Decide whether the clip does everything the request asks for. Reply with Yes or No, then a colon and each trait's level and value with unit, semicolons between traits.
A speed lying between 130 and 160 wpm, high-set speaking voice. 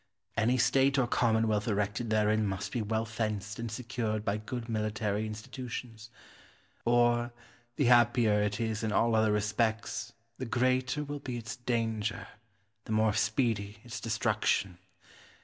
No: average, 140 wpm; low, 110 Hz